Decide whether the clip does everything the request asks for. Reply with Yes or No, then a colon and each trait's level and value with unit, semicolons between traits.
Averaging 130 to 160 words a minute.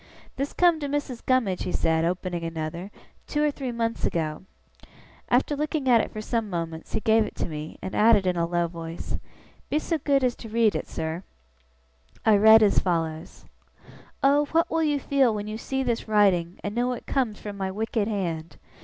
No: average, 195 wpm